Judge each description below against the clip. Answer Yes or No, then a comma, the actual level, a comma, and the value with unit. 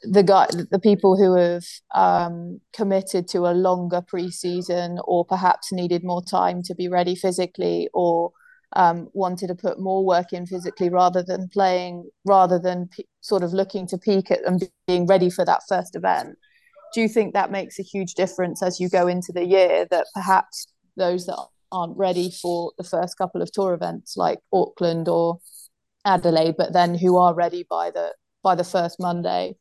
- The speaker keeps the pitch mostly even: Yes, narrow, 1.4 semitones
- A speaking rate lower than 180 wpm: No, average, 185 wpm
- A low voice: No, medium, 180 Hz